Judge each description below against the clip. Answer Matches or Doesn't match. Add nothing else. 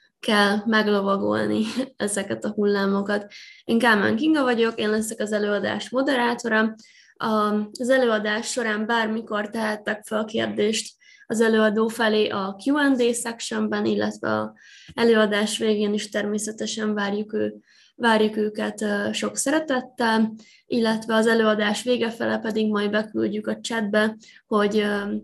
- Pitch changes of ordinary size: Doesn't match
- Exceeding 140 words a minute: Doesn't match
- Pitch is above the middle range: Matches